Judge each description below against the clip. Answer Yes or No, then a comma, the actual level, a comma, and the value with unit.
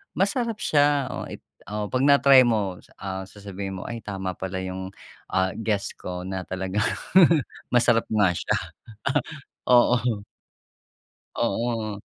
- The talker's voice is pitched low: Yes, low, 105 Hz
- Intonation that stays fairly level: No, average, 4.4 semitones